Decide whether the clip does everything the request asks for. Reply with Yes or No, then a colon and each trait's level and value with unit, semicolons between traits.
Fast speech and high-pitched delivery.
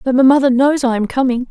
Yes: fast, 280 wpm; very high, 260 Hz